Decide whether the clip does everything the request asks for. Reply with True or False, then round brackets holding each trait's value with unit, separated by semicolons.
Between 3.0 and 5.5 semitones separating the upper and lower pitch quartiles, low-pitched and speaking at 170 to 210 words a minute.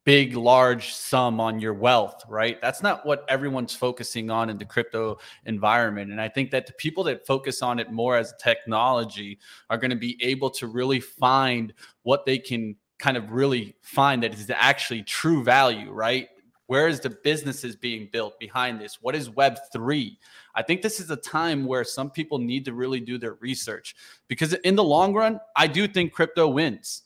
True (3.4 semitones; 125 Hz; 195 wpm)